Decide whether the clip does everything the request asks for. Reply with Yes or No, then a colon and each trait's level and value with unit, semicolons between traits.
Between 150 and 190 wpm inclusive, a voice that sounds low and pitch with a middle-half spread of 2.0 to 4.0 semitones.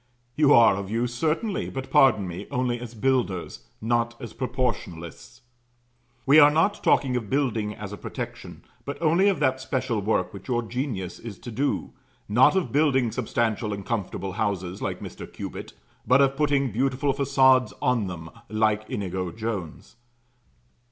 No: average, 160 wpm; low, 120 Hz; average, 4.4 semitones